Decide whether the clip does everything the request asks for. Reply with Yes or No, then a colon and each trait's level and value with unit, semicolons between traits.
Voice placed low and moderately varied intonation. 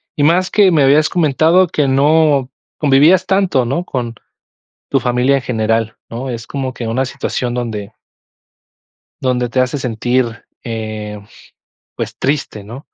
Yes: low, 130 Hz; average, 4.0 semitones